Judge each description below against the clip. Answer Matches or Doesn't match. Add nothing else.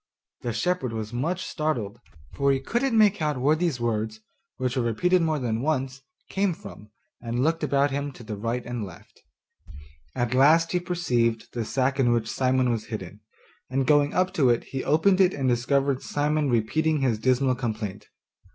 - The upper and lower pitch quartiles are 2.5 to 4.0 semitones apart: Doesn't match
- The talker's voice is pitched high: Doesn't match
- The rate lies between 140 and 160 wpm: Doesn't match